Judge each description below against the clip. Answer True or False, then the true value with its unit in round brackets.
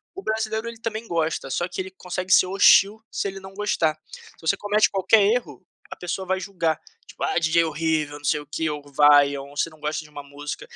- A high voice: False (170 Hz)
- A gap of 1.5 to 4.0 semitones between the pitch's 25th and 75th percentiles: False (4.9 semitones)